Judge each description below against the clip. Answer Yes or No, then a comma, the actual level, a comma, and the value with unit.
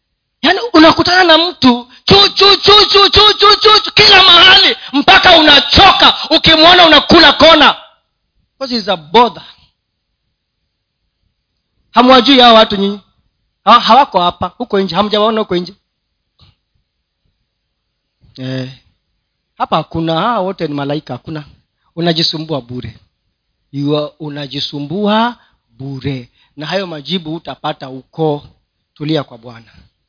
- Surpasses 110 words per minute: No, slow, 100 wpm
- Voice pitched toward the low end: No, high, 190 Hz